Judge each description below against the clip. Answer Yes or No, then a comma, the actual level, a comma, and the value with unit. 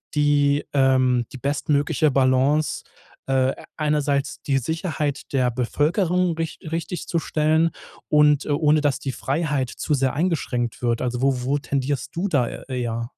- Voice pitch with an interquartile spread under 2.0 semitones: No, average, 2.9 semitones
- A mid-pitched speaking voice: Yes, medium, 145 Hz